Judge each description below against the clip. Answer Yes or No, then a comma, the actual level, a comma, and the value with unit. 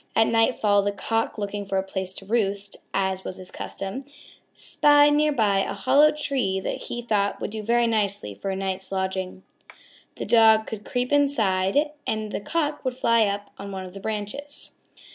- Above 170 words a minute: Yes, average, 180 wpm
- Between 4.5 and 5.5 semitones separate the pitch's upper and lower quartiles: No, average, 3.7 semitones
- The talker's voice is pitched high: Yes, high, 205 Hz